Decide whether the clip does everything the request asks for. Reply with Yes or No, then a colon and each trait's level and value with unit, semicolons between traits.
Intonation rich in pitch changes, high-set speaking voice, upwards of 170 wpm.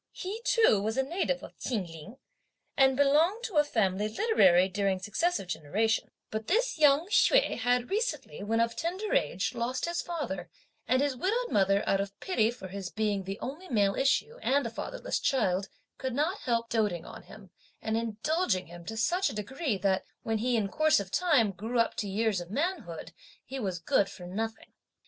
Yes: wide, 7.8 semitones; high, 230 Hz; average, 190 wpm